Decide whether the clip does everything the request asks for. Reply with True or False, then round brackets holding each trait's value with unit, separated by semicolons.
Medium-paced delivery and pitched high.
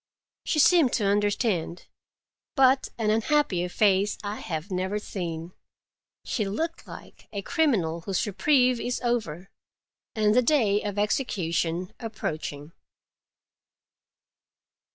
False (110 wpm; 205 Hz)